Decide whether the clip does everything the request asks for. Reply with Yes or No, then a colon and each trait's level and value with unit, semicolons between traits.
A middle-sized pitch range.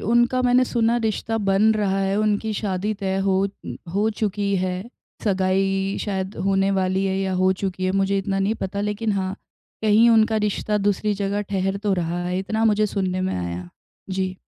No: narrow, 1.9 semitones